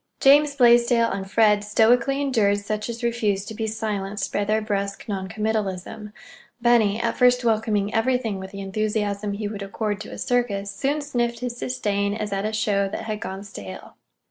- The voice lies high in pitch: Yes, high, 215 Hz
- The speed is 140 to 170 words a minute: No, average, 180 wpm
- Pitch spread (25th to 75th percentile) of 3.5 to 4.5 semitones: No, average, 2.8 semitones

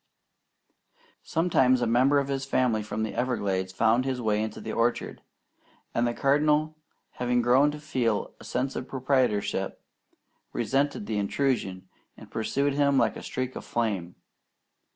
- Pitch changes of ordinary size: Yes, average, 3.9 semitones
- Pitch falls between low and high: No, low, 125 Hz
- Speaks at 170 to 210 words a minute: No, average, 150 wpm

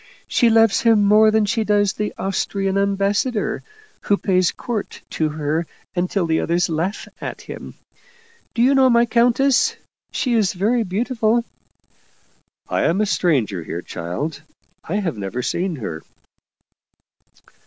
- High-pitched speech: Yes, high, 200 Hz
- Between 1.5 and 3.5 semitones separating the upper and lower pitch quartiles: No, average, 5.3 semitones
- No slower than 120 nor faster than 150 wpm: Yes, average, 145 wpm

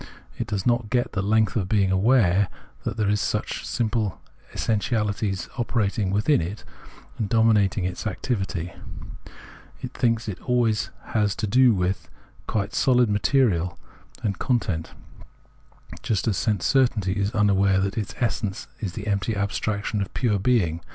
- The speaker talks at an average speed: Yes, average, 145 wpm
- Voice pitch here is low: Yes, low, 105 Hz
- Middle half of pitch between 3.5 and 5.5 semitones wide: No, average, 2.8 semitones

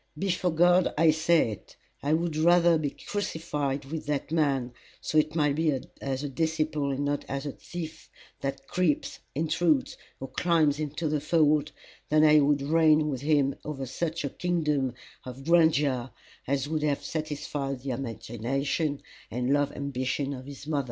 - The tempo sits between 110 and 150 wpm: No, average, 165 wpm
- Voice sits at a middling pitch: Yes, medium, 150 Hz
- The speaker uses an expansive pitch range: No, narrow, 2.6 semitones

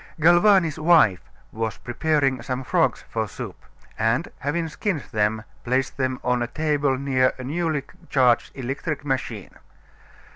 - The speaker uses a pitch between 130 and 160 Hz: Yes, low, 135 Hz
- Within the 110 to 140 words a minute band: Yes, slow, 135 wpm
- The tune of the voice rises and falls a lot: No, average, 4.0 semitones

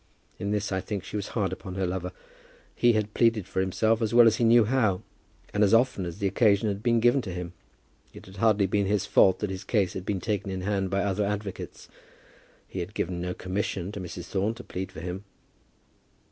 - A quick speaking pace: Yes, fast, 225 wpm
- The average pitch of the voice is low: Yes, low, 100 Hz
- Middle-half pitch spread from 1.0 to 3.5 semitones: Yes, narrow, 2.4 semitones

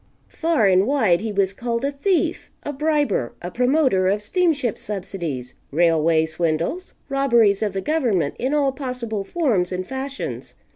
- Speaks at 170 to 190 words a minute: No, average, 150 wpm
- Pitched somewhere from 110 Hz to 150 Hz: No, high, 220 Hz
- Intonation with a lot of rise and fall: Yes, wide, 7.0 semitones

